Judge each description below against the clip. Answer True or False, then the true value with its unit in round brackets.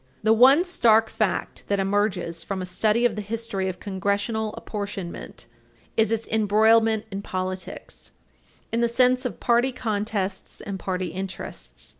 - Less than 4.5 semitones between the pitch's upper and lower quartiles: True (3.0 semitones)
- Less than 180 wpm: True (145 wpm)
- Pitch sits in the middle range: False (210 Hz)